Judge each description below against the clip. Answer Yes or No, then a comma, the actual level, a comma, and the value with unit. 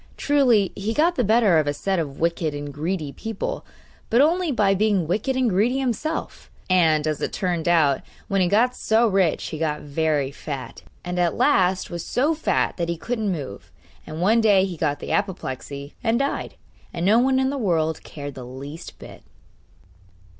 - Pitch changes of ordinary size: No, wide, 6.4 semitones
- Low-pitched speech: No, medium, 185 Hz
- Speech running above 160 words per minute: Yes, average, 190 wpm